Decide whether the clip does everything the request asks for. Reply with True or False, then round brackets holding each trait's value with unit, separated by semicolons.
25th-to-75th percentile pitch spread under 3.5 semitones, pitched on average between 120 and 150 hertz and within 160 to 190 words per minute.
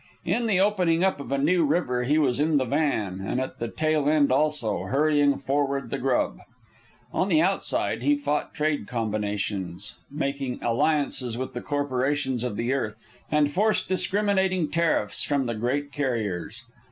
False (4.2 semitones; 140 Hz; 165 wpm)